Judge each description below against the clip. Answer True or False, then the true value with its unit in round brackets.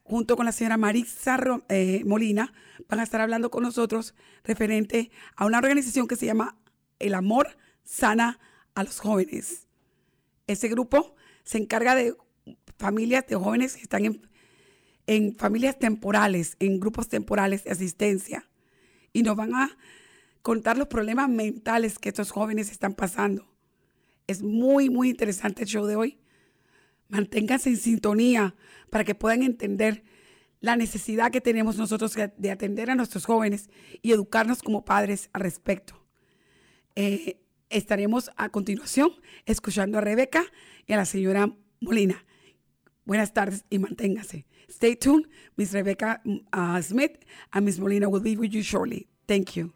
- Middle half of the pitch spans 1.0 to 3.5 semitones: True (2.6 semitones)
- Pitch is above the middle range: True (220 Hz)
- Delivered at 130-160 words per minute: True (145 wpm)